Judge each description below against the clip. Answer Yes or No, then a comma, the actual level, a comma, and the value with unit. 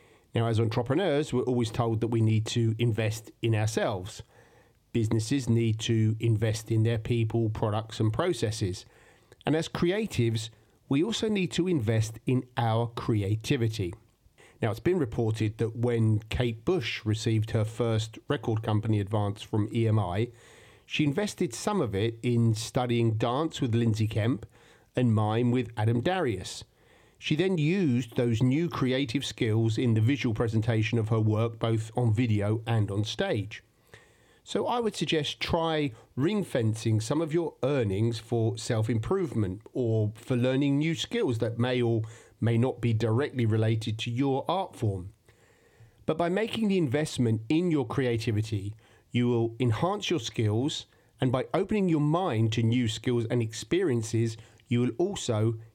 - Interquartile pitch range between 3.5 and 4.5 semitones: No, average, 2.9 semitones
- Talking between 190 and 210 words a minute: No, average, 155 wpm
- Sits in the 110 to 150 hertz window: Yes, low, 115 Hz